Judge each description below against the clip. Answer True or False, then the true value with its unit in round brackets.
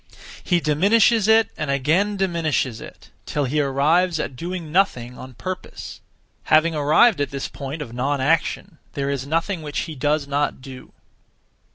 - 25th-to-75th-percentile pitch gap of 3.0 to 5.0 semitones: True (4.1 semitones)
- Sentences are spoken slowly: False (165 wpm)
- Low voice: False (150 Hz)